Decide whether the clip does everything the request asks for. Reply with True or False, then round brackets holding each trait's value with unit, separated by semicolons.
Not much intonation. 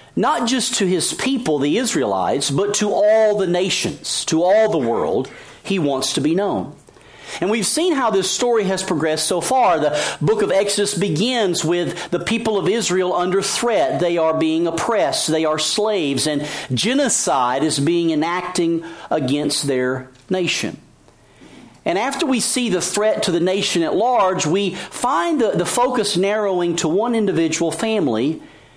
False (4.8 semitones)